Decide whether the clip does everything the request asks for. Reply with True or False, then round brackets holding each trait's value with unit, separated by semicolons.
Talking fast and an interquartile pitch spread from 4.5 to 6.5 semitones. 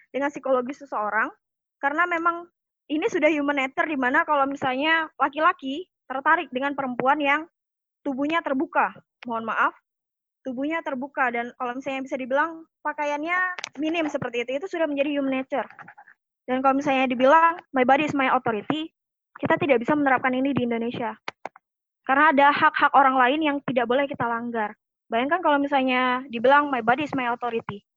False (155 wpm; 3.1 semitones)